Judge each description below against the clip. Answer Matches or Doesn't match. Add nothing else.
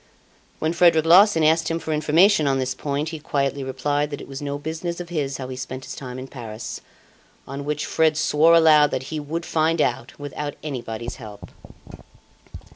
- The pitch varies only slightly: Doesn't match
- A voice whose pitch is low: Doesn't match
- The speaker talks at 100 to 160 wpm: Doesn't match